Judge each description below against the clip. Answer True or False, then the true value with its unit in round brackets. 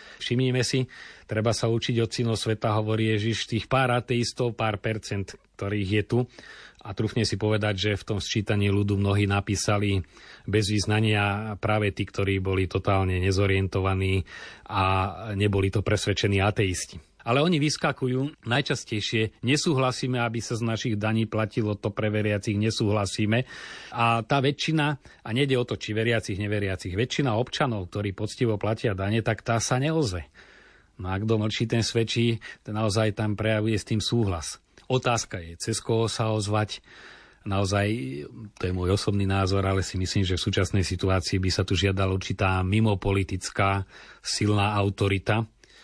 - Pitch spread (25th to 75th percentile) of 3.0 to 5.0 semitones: False (2.6 semitones)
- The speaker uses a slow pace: False (150 wpm)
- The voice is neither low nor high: False (110 Hz)